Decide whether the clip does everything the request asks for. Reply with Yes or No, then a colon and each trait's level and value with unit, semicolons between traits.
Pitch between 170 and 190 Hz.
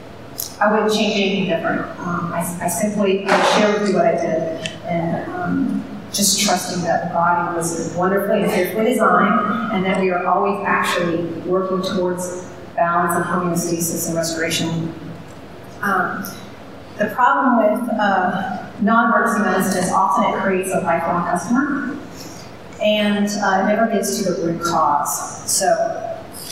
Yes: medium, 185 Hz